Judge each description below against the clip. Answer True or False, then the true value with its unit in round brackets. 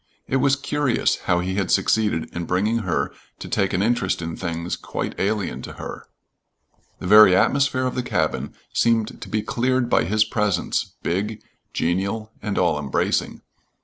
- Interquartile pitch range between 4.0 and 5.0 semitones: True (4.4 semitones)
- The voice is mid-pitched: False (105 Hz)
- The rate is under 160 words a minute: False (165 wpm)